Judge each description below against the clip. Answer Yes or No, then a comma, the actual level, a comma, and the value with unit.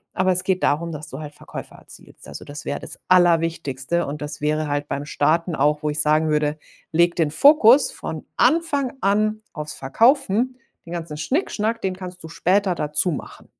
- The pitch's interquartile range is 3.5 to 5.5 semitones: Yes, average, 4.7 semitones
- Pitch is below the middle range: No, medium, 165 Hz